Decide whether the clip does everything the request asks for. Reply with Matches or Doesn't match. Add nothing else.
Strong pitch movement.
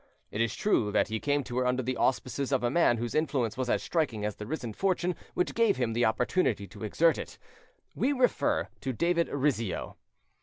Matches